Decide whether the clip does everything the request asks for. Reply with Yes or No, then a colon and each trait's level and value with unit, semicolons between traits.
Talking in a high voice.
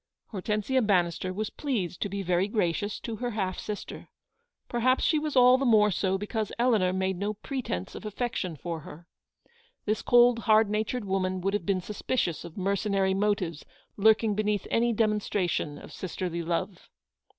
Yes: high, 205 Hz